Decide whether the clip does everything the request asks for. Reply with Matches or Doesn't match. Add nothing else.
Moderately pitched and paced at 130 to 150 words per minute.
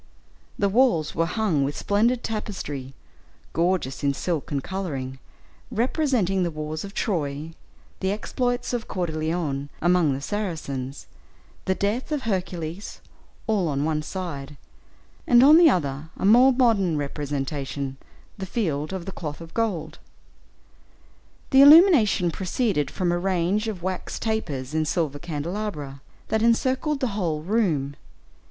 Matches